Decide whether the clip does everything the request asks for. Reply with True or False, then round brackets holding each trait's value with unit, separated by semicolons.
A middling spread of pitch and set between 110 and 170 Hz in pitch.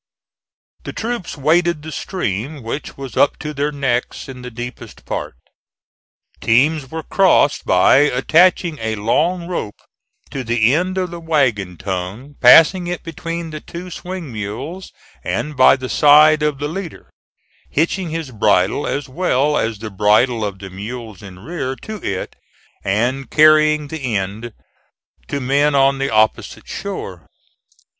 False (6.1 semitones; 140 Hz)